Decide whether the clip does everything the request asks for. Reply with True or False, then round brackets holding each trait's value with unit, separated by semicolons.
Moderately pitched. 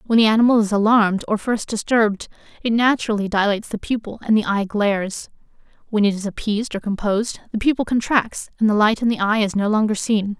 False (215 Hz)